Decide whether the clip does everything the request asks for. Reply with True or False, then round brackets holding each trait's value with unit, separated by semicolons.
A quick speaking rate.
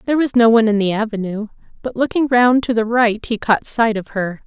True (240 wpm)